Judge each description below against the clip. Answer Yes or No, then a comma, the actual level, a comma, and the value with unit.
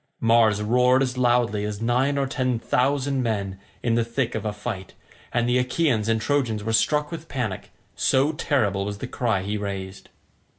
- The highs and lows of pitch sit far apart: No, average, 3.8 semitones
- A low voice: Yes, low, 120 Hz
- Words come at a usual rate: Yes, average, 180 wpm